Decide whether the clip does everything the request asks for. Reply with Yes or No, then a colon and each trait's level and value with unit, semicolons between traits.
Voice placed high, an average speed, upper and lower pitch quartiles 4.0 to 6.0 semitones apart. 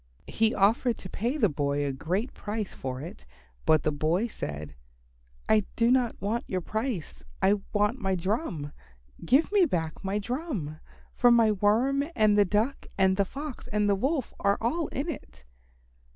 Yes: high, 210 Hz; average, 170 wpm; wide, 5.4 semitones